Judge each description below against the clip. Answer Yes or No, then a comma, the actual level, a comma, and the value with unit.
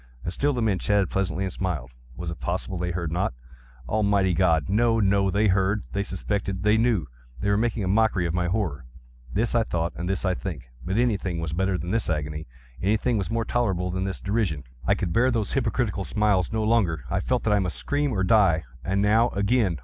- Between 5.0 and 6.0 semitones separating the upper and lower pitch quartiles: No, average, 3.8 semitones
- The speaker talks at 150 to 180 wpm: No, average, 200 wpm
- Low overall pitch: Yes, very low, 95 Hz